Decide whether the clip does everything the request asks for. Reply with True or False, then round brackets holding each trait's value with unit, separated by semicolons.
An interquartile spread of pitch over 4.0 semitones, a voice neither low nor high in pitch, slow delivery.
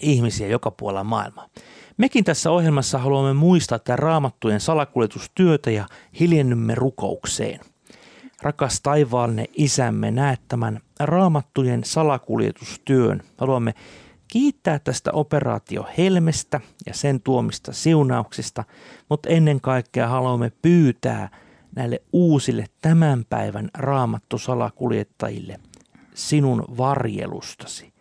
False (4.7 semitones; 130 Hz; 90 wpm)